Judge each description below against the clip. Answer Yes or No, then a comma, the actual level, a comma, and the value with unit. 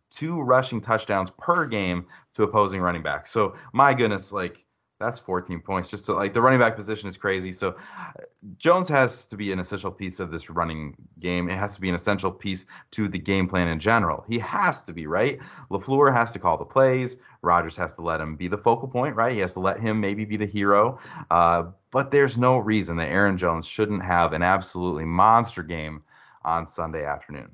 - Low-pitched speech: Yes, very low, 95 Hz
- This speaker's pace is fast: Yes, fast, 210 wpm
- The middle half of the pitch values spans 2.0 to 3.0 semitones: No, average, 4.6 semitones